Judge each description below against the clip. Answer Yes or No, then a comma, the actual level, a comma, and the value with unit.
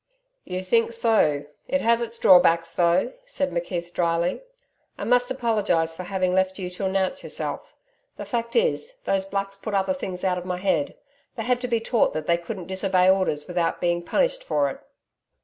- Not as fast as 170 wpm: No, average, 185 wpm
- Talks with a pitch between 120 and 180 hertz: No, high, 190 Hz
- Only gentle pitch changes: No, average, 4.7 semitones